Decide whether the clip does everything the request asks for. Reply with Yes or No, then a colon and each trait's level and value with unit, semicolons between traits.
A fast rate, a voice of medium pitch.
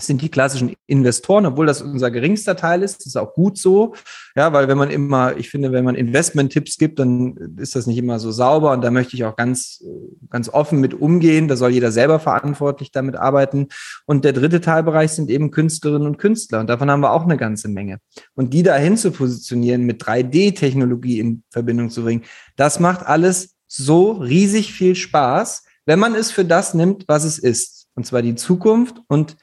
Yes: fast, 200 wpm; medium, 145 Hz